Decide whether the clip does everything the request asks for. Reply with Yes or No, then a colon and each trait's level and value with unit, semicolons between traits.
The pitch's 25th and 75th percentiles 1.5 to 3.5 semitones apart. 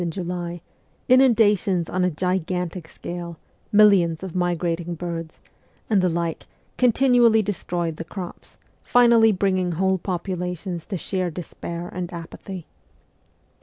Yes: narrow, 2.5 semitones